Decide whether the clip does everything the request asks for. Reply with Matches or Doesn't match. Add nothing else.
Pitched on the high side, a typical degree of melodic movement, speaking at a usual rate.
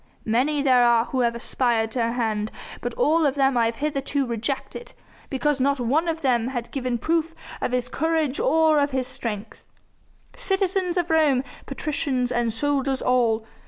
Matches